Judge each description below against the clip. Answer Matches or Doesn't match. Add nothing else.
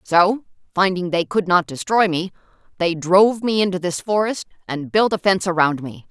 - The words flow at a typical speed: Matches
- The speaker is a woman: Matches